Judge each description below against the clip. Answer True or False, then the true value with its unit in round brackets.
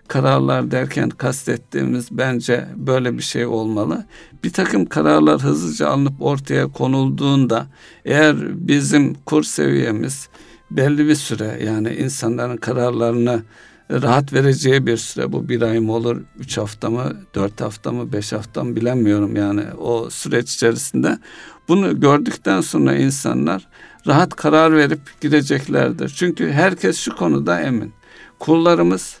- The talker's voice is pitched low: True (120 Hz)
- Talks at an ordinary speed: True (125 wpm)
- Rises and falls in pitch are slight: False (4.3 semitones)